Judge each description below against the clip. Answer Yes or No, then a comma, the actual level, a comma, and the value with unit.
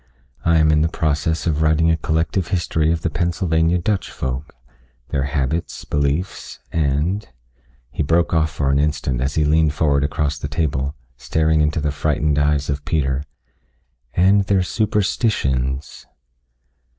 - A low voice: Yes, very low, 75 Hz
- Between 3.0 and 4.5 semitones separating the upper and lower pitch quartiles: No, narrow, 2.6 semitones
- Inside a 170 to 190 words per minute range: No, average, 155 wpm